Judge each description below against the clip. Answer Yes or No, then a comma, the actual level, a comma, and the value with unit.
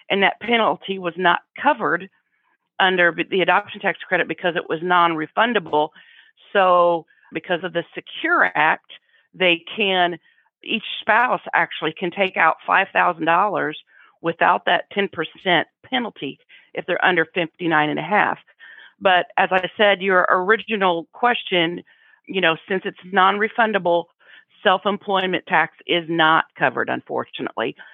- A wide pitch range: No, narrow, 2.6 semitones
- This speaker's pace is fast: No, slow, 135 wpm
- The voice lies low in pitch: No, medium, 180 Hz